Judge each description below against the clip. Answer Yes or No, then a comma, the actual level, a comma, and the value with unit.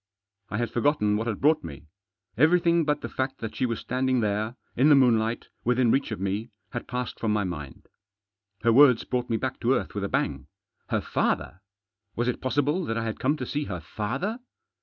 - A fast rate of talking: Yes, fast, 210 wpm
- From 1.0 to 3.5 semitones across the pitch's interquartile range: No, average, 4.2 semitones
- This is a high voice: No, low, 120 Hz